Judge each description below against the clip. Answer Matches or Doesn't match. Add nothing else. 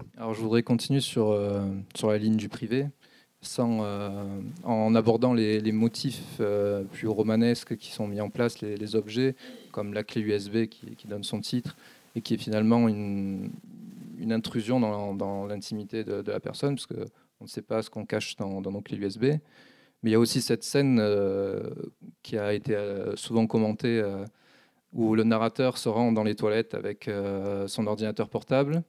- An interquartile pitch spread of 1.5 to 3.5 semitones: Matches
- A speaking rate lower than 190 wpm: Doesn't match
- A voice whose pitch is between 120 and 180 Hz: Doesn't match